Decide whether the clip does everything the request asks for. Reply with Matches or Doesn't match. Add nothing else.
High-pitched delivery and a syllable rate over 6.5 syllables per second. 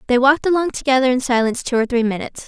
Matches